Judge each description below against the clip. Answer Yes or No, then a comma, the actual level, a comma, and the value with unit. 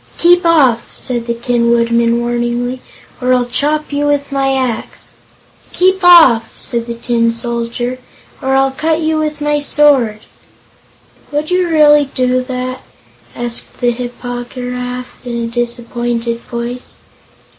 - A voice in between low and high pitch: No, very high, 250 Hz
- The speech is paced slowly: No, average, 145 wpm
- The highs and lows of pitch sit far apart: No, average, 3.5 semitones